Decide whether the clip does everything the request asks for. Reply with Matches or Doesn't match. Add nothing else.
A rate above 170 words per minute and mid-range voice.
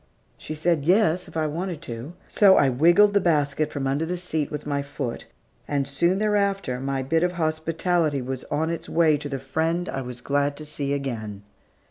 Matches